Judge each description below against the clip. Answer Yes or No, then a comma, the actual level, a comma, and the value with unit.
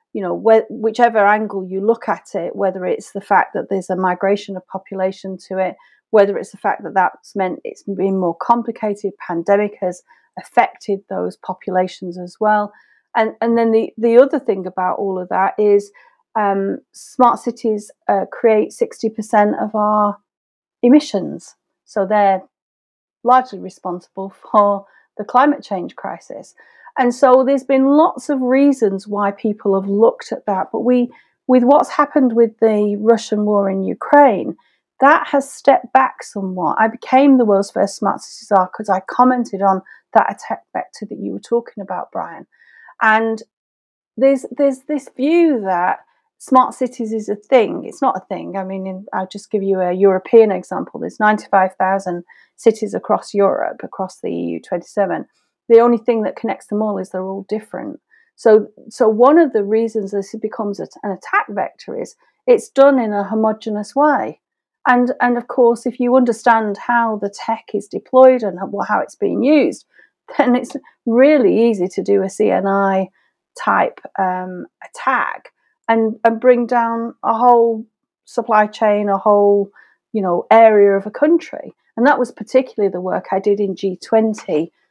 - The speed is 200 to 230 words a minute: No, average, 165 wpm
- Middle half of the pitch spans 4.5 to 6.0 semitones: No, average, 3.9 semitones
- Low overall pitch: No, high, 215 Hz